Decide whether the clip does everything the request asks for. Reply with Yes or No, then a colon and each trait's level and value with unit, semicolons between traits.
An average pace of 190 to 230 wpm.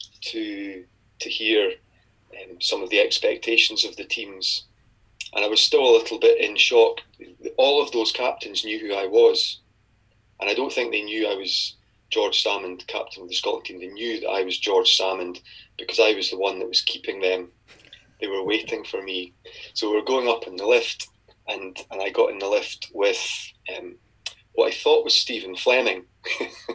Yes: average, 195 wpm